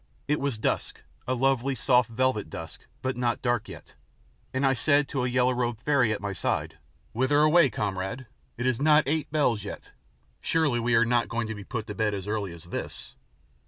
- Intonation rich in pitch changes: No, average, 3.9 semitones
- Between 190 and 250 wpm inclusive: Yes, average, 200 wpm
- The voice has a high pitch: No, low, 120 Hz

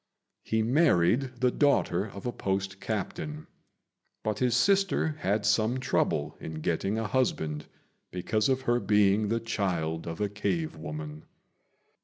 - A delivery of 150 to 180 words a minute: No, average, 140 wpm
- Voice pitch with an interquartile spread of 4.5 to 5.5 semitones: Yes, average, 5.2 semitones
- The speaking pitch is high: No, low, 110 Hz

